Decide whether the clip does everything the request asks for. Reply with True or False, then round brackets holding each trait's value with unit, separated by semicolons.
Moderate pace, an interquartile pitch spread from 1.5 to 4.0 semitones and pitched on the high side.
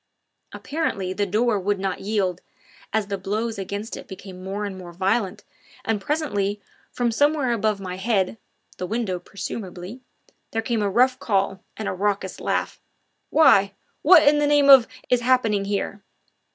True (160 wpm; 3.7 semitones; 205 Hz)